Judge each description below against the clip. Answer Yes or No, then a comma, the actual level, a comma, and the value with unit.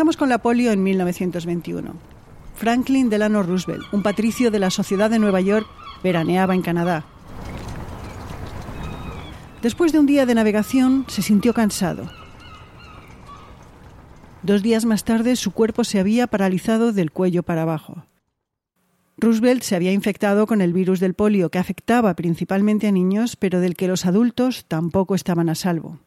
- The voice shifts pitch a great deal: No, average, 4.1 semitones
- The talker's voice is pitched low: No, high, 200 Hz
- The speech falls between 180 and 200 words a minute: No, average, 150 wpm